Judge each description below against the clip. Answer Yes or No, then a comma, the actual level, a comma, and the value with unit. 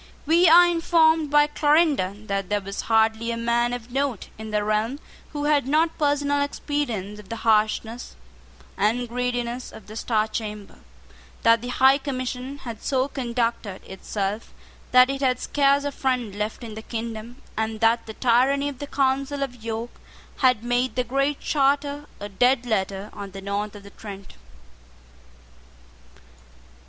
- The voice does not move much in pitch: No, average, 4.3 semitones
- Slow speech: No, average, 160 wpm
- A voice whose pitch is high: Yes, high, 245 Hz